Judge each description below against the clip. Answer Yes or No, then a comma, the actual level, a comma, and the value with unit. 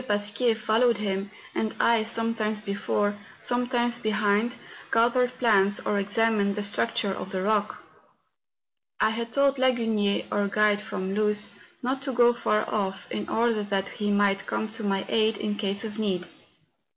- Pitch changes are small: Yes, narrow, 2.3 semitones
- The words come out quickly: No, average, 155 wpm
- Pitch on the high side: Yes, high, 215 Hz